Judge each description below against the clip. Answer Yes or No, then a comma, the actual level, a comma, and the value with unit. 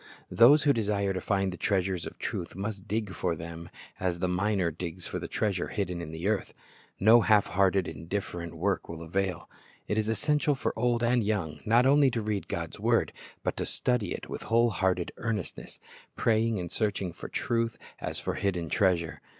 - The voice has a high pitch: No, low, 100 Hz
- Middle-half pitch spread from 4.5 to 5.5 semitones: No, average, 4.1 semitones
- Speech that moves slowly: No, average, 190 wpm